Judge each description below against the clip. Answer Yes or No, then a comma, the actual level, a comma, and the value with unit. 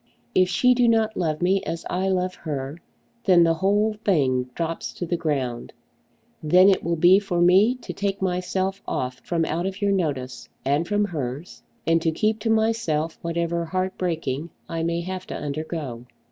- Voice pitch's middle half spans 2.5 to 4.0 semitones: Yes, average, 3.5 semitones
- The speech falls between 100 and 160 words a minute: No, average, 180 wpm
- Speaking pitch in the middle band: Yes, medium, 175 Hz